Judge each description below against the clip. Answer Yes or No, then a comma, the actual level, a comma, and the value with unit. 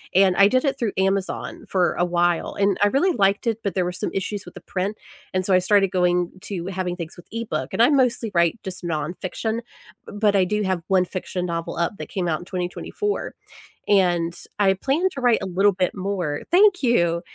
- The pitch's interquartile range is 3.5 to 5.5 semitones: No, average, 2.9 semitones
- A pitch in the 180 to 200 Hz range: Yes, high, 190 Hz